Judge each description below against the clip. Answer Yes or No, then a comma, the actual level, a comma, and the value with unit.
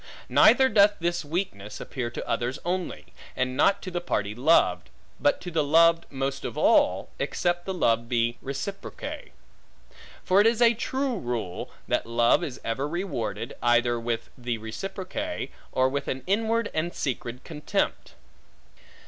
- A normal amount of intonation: No, wide, 7.9 semitones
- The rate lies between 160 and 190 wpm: No, average, 150 wpm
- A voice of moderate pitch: Yes, medium, 150 Hz